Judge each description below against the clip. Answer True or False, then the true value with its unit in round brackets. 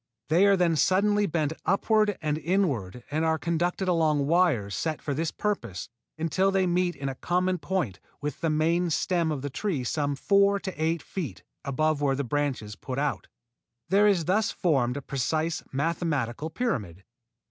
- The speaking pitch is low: False (160 Hz)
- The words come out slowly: False (170 wpm)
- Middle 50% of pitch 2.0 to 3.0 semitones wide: False (4.5 semitones)